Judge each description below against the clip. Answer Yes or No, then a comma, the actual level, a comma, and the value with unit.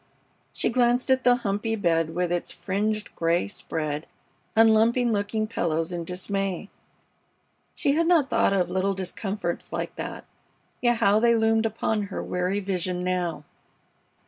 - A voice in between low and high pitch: No, high, 200 Hz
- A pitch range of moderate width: Yes, average, 3.9 semitones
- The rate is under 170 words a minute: Yes, average, 145 wpm